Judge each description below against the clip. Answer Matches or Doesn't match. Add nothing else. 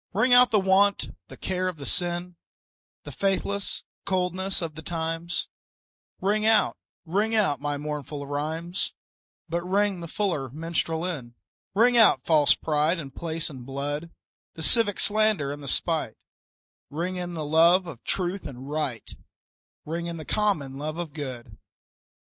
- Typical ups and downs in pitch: Matches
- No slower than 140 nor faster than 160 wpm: Matches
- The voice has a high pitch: Doesn't match